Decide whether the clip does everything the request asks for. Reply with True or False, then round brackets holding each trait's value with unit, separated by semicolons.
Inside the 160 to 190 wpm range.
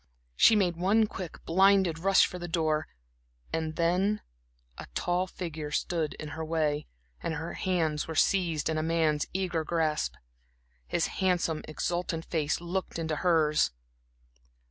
False (145 wpm)